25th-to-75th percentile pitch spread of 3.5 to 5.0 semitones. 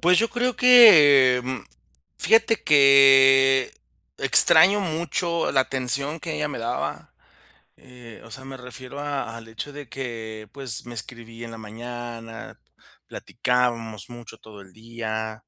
Yes: average, 3.9 semitones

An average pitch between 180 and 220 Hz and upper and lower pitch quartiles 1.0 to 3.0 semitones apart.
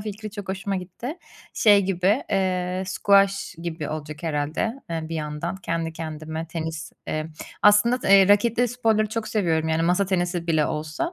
No: medium, 185 Hz; average, 4.2 semitones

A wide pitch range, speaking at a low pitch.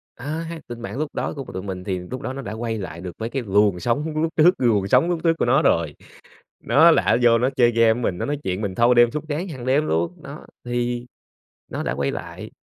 Yes: wide, 5.8 semitones; low, 120 Hz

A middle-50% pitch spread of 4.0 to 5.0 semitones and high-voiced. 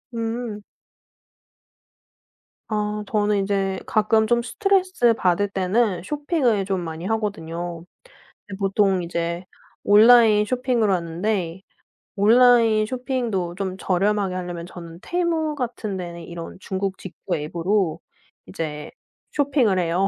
Yes: average, 4.5 semitones; high, 200 Hz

